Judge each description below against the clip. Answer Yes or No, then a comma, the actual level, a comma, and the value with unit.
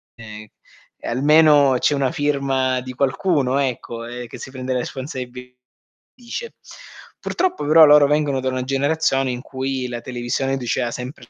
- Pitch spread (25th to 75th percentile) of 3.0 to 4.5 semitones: No, narrow, 2.4 semitones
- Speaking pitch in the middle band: No, low, 130 Hz